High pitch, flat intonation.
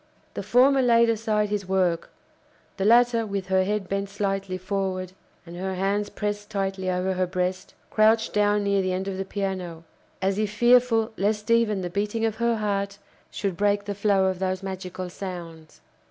Yes: high, 200 Hz; narrow, 2.1 semitones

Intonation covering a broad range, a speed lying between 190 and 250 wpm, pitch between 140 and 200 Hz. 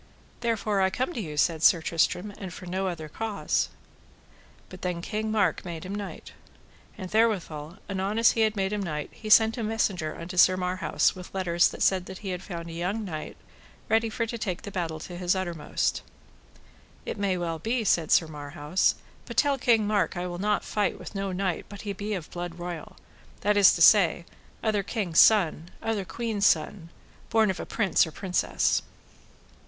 No: average, 3.5 semitones; average, 195 wpm; high, 190 Hz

